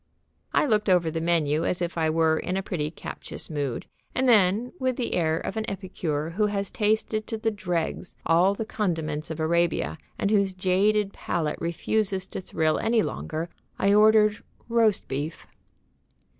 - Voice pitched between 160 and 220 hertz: Yes, medium, 185 Hz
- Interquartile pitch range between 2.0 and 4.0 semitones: No, average, 4.6 semitones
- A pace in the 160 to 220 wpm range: Yes, average, 170 wpm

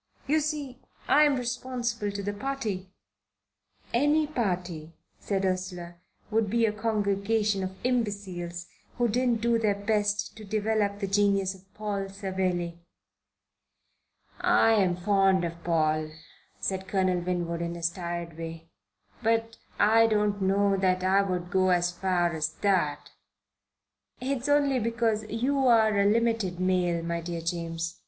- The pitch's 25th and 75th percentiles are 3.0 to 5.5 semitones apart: Yes, average, 4.2 semitones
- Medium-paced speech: No, slow, 130 wpm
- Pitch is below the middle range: No, high, 200 Hz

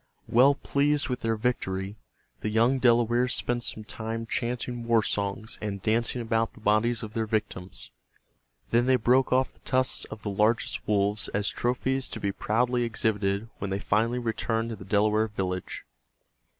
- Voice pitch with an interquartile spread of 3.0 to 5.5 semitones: No, narrow, 2.5 semitones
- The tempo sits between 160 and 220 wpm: Yes, average, 165 wpm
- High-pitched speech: No, low, 115 Hz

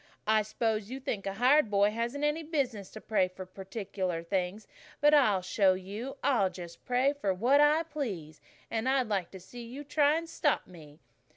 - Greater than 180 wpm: Yes, average, 190 wpm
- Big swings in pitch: Yes, wide, 6.4 semitones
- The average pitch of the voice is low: No, high, 220 Hz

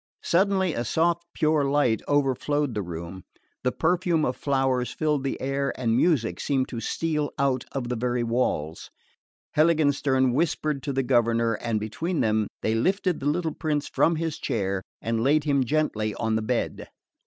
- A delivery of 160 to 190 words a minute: Yes, average, 165 wpm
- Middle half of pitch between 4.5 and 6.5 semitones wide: Yes, average, 4.9 semitones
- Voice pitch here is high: No, low, 135 Hz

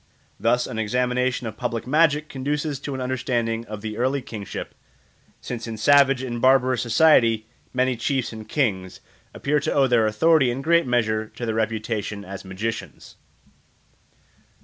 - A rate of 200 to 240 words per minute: No, average, 150 wpm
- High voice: No, low, 120 Hz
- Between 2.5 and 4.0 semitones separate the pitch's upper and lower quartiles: Yes, average, 3.3 semitones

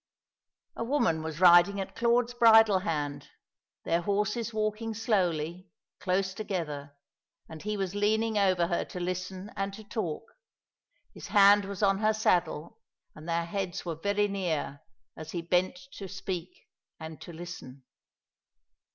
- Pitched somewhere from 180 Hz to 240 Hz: Yes, high, 190 Hz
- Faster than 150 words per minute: No, average, 145 wpm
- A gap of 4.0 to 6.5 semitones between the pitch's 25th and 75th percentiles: No, average, 3.6 semitones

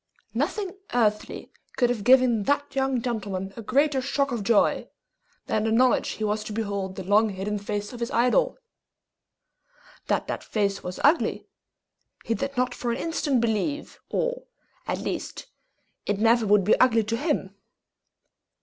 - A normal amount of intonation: Yes, average, 4.3 semitones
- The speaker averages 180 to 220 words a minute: No, average, 160 wpm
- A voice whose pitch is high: Yes, high, 230 Hz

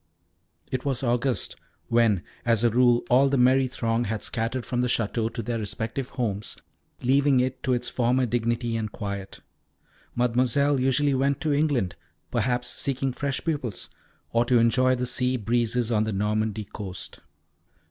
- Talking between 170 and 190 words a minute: No, average, 160 wpm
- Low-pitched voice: Yes, low, 120 Hz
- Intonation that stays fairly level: Yes, narrow, 2.2 semitones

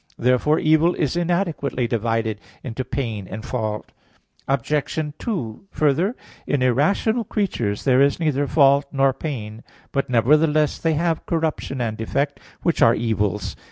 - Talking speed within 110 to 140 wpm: Yes, slow, 135 wpm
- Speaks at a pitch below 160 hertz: Yes, medium, 140 Hz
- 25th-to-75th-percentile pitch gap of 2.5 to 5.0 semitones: No, wide, 5.4 semitones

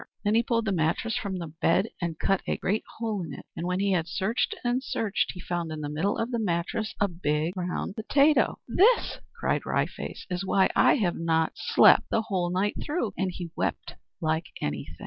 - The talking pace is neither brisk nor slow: No, fast, 210 wpm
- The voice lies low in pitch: No, medium, 185 Hz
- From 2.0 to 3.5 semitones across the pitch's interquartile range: No, average, 4.7 semitones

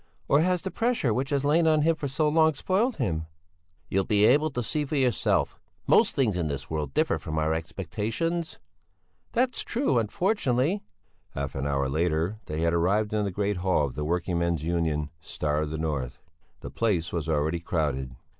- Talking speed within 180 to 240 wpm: Yes, average, 190 wpm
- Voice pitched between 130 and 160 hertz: No, very low, 95 Hz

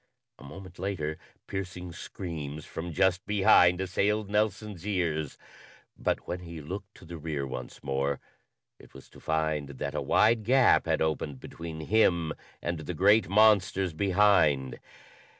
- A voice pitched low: Yes, very low, 90 Hz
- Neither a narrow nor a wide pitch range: Yes, average, 4.2 semitones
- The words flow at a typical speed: Yes, average, 145 wpm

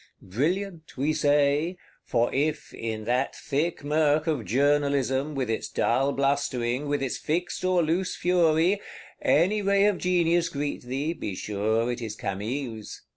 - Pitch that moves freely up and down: No, average, 4.8 semitones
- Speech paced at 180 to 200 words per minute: No, average, 145 wpm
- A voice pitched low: No, medium, 145 Hz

